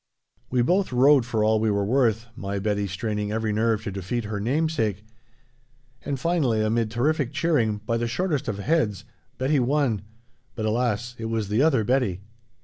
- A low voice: Yes, low, 115 Hz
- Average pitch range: Yes, average, 4.1 semitones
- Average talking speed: Yes, average, 170 wpm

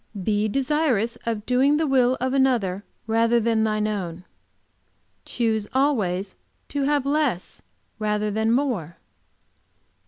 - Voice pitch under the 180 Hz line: No, high, 230 Hz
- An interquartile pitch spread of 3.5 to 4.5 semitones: Yes, average, 4.1 semitones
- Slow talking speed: Yes, slow, 120 wpm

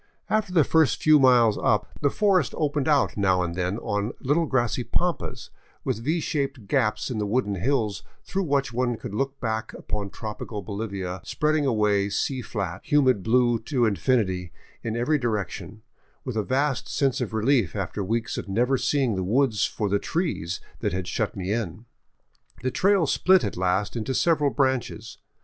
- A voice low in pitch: Yes, low, 120 Hz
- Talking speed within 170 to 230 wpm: Yes, average, 175 wpm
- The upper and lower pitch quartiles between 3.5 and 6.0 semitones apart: Yes, average, 5.2 semitones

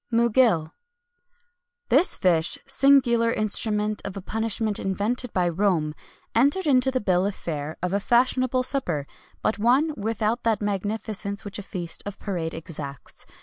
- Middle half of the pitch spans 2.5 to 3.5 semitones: No, average, 4.5 semitones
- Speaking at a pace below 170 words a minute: Yes, average, 150 wpm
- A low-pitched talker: No, high, 210 Hz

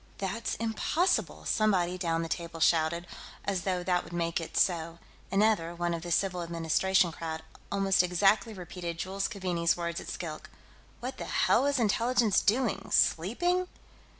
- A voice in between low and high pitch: Yes, medium, 180 Hz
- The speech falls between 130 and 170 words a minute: Yes, average, 150 wpm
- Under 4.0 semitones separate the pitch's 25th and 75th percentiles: Yes, average, 3.4 semitones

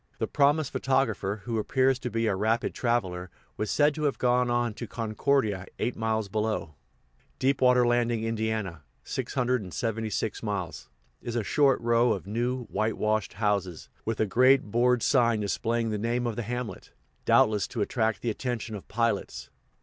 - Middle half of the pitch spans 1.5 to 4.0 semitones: Yes, narrow, 2.5 semitones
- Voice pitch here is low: Yes, low, 115 Hz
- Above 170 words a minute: No, average, 160 wpm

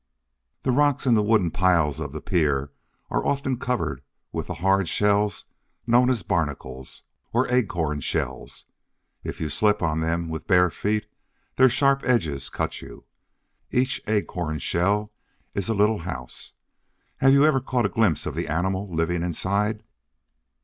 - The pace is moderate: Yes, average, 155 wpm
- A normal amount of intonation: No, wide, 6.3 semitones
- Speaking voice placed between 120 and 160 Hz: No, low, 100 Hz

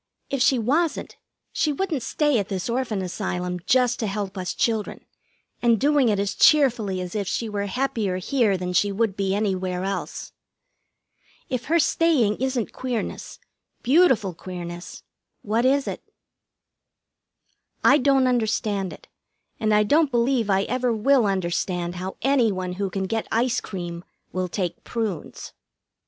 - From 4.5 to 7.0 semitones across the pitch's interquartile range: Yes, average, 5.1 semitones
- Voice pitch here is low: No, high, 215 Hz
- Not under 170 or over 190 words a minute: No, average, 150 wpm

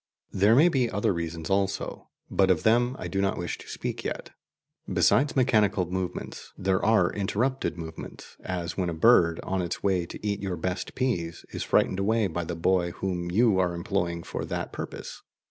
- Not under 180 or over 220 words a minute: Yes, average, 185 wpm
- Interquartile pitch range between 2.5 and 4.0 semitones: Yes, average, 3.5 semitones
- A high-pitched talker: No, very low, 95 Hz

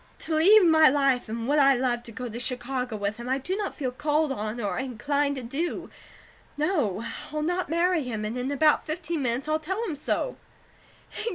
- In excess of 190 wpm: Yes, average, 200 wpm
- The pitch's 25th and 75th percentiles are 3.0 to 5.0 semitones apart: Yes, average, 4.4 semitones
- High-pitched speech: Yes, very high, 275 Hz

